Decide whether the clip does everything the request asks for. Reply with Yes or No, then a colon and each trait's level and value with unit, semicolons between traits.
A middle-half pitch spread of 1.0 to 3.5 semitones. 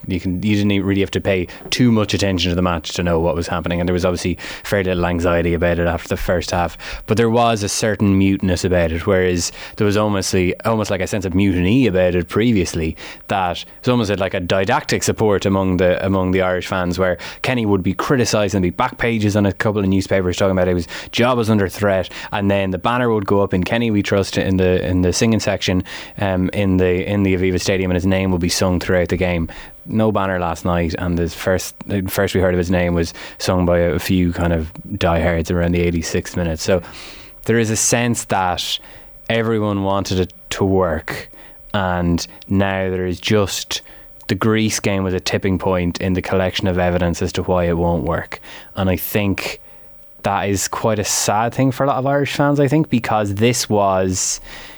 Yes: average, 2.7 semitones